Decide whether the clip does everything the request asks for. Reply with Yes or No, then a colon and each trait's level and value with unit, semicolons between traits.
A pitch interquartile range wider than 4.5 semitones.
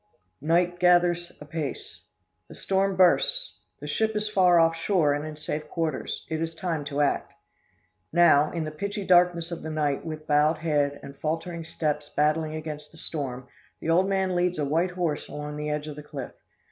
No: average, 2.9 semitones